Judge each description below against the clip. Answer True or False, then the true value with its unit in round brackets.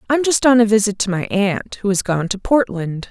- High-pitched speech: True (215 Hz)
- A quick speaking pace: True (250 wpm)